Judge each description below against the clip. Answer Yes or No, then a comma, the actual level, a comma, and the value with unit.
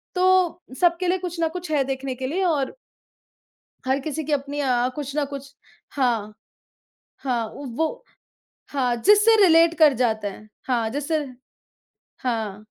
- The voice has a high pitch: Yes, very high, 280 Hz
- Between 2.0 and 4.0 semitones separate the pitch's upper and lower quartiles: No, average, 5.0 semitones